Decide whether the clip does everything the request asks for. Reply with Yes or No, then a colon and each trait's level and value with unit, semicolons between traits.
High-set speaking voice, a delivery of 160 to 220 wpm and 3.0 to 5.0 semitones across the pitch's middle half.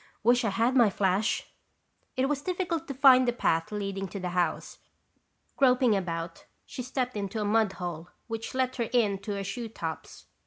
Yes: high, 220 Hz; average, 180 wpm; average, 4.6 semitones